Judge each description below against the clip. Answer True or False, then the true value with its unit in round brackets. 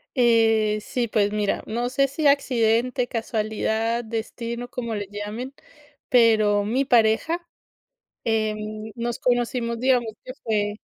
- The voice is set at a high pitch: True (230 Hz)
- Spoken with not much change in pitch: True (2.2 semitones)